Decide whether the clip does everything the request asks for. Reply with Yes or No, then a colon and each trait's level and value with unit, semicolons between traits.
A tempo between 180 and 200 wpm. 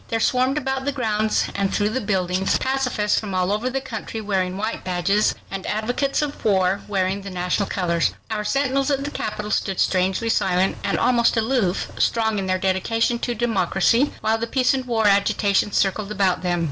Yes: average, 185 wpm